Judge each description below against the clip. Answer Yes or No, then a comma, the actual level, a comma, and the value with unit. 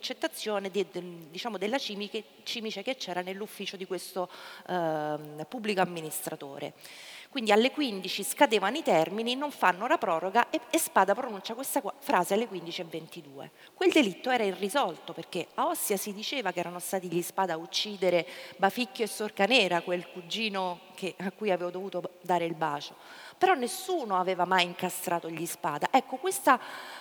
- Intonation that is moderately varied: Yes, average, 5.0 semitones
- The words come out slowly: No, average, 150 wpm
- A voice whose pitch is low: No, high, 195 Hz